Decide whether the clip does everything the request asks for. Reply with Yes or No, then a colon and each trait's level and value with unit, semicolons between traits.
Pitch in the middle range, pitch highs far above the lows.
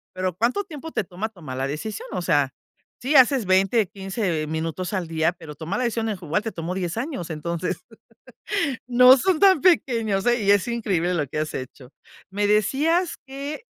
No: high, 195 Hz; wide, 6.3 semitones